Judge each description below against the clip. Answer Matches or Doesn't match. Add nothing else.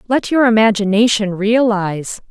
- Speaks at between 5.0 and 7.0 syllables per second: Doesn't match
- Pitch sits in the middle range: Doesn't match